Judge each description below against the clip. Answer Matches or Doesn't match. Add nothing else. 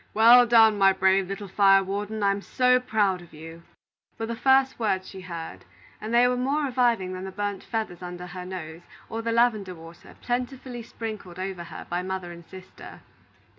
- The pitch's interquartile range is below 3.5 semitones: Doesn't match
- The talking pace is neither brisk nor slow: Matches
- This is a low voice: Doesn't match